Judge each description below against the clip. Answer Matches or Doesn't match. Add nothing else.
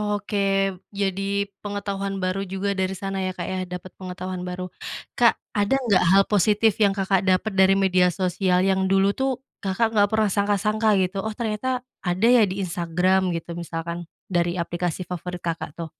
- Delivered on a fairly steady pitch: Matches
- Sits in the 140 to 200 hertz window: Matches